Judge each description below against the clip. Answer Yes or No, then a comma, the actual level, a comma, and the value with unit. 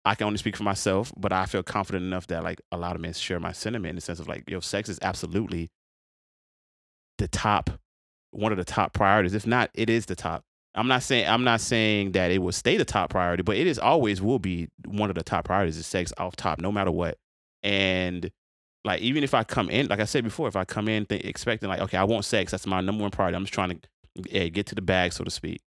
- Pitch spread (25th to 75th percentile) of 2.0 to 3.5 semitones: Yes, average, 3.1 semitones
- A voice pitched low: Yes, very low, 95 Hz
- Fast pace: Yes, fast, 260 wpm